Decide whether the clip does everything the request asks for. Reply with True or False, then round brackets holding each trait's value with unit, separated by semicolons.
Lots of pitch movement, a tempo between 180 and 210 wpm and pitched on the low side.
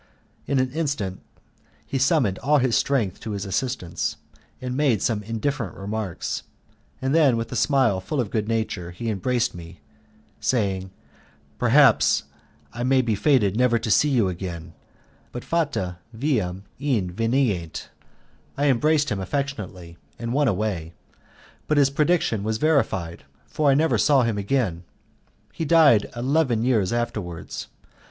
False (5.9 semitones; 140 wpm; 115 Hz)